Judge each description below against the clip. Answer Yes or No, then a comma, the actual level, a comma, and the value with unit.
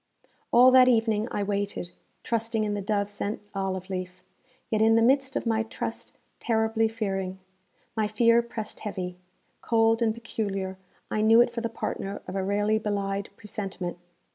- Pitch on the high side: Yes, high, 215 Hz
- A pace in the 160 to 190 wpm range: Yes, average, 165 wpm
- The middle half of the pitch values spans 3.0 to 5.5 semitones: No, narrow, 2.4 semitones